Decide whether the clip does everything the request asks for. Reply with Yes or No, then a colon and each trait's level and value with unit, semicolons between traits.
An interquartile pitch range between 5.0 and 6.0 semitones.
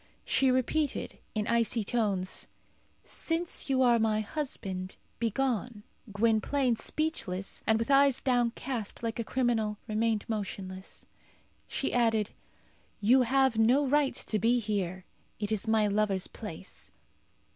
No: average, 3.6 semitones